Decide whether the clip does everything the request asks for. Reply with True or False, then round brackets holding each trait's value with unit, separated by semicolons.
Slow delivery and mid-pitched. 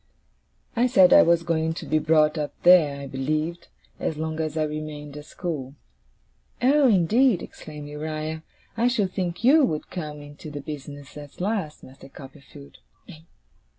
False (155 wpm; 155 Hz)